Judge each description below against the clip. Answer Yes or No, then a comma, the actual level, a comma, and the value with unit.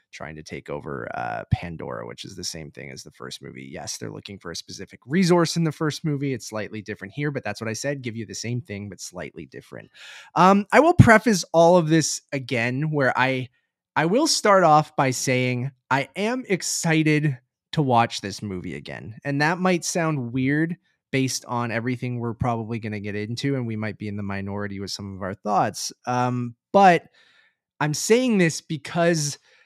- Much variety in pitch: Yes, wide, 7.1 semitones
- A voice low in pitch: Yes, low, 130 Hz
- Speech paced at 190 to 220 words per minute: Yes, average, 200 wpm